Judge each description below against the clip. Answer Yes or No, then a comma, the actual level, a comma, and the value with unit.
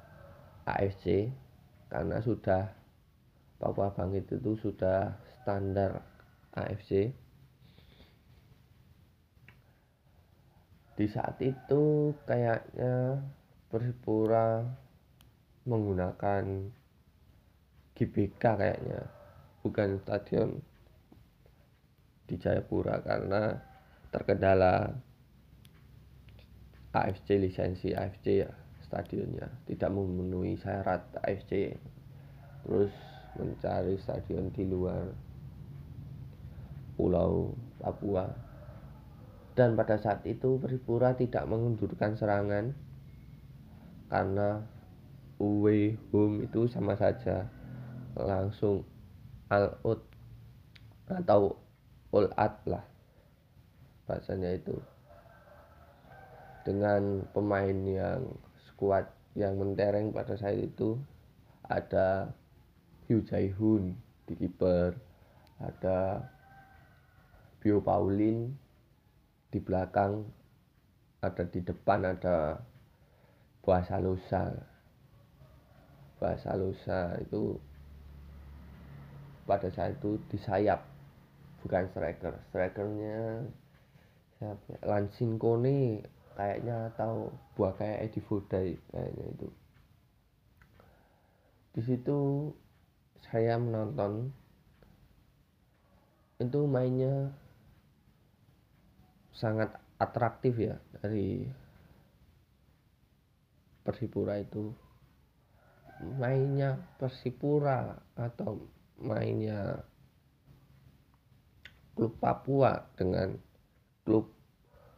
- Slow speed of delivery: Yes, slow, 65 wpm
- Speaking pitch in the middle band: No, low, 105 Hz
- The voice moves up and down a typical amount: Yes, average, 4.1 semitones